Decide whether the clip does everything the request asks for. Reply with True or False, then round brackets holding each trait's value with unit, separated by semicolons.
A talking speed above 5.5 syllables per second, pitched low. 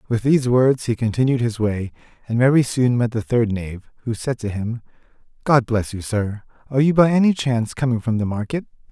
True (5.7 syllables/s; 120 Hz)